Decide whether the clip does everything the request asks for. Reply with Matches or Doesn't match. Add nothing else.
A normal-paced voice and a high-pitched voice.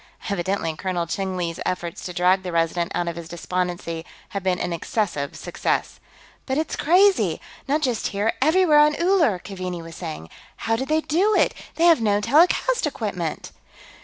Matches